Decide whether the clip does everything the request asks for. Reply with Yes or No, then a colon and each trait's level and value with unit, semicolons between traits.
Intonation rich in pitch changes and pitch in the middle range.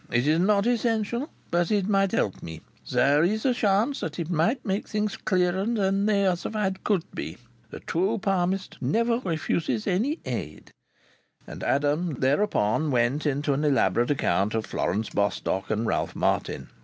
Yes: wide, 7.1 semitones; medium, 180 Hz